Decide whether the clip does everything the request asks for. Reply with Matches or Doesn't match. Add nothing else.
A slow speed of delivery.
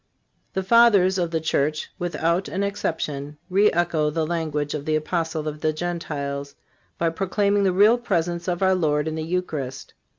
Doesn't match